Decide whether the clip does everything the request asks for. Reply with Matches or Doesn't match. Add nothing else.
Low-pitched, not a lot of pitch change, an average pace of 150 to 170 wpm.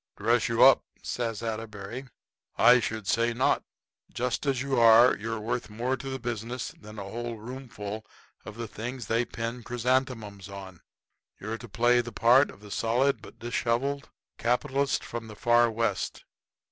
Matches